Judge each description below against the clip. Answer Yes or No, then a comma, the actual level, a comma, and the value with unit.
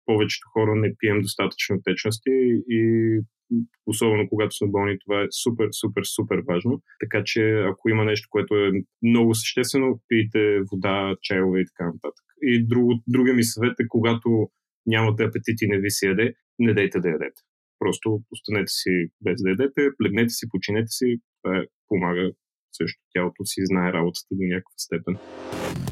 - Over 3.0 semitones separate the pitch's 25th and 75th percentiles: No, average, 2.7 semitones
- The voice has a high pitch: No, low, 110 Hz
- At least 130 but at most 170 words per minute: Yes, average, 160 wpm